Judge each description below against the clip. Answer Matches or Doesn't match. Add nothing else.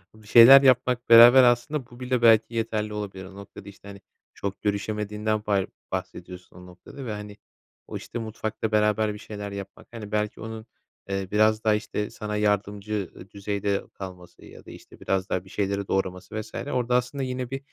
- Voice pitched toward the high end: Doesn't match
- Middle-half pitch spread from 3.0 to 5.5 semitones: Doesn't match